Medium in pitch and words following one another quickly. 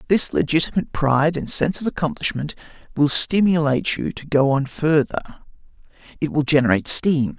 No: medium, 150 Hz; average, 145 wpm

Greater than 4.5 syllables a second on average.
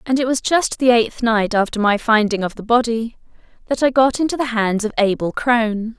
Yes: 5.3 syllables/s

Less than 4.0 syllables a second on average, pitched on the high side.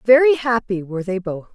No: 5.8 syllables/s; high, 220 Hz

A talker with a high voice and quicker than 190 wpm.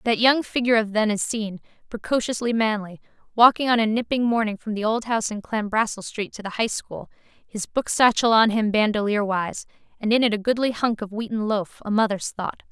Yes: high, 220 Hz; average, 200 wpm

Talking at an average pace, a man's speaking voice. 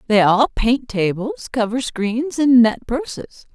No: average, 150 wpm; female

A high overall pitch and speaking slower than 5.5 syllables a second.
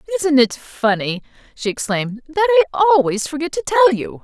No: very high, 290 Hz; 5.6 syllables/s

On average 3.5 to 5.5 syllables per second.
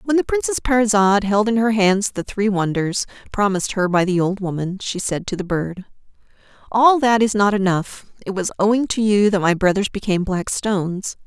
Yes: 5.3 syllables/s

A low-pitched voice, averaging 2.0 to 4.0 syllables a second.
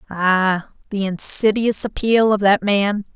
No: high, 200 Hz; 3.7 syllables/s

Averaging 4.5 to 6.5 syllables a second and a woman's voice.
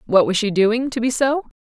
Yes: 5.3 syllables/s; female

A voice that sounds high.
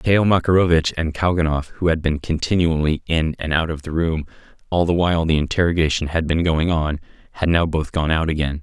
No: very low, 80 Hz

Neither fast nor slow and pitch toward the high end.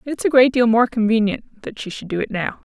No: fast, 265 wpm; high, 230 Hz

